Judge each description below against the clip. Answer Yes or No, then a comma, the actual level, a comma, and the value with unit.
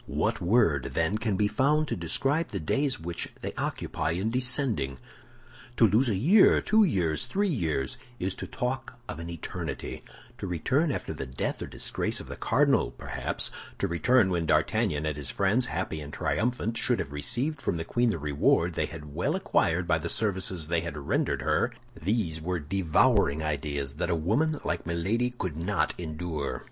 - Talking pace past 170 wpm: Yes, average, 180 wpm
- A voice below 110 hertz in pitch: Yes, very low, 90 Hz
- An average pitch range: No, wide, 7.7 semitones